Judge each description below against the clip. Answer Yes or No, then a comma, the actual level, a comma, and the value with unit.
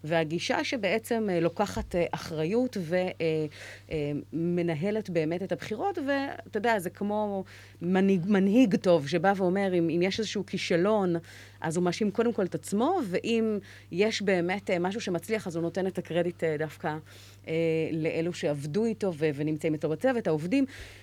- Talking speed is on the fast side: No, average, 135 wpm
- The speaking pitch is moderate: Yes, medium, 180 Hz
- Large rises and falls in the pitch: No, average, 4.5 semitones